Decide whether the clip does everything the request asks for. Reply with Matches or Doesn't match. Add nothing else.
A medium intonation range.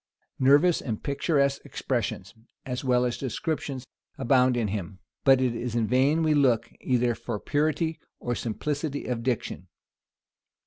Matches